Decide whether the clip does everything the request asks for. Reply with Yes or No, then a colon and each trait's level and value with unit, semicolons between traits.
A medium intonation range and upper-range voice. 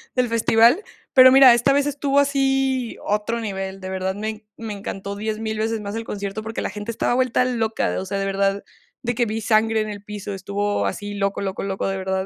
Yes: average, 3.2 semitones; high, 215 Hz